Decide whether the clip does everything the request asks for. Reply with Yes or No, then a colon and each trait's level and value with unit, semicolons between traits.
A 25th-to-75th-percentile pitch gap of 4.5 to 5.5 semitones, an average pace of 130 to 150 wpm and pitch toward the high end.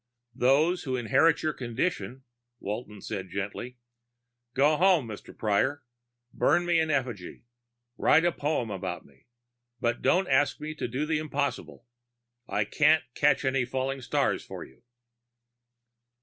No: average, 5.1 semitones; slow, 135 wpm; low, 135 Hz